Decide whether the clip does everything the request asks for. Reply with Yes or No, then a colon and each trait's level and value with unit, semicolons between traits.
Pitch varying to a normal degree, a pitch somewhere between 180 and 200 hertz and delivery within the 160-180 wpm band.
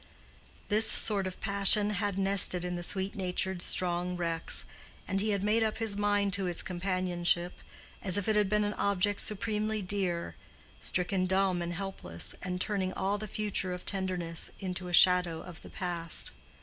No: narrow, 2.3 semitones; high, 190 Hz; average, 175 wpm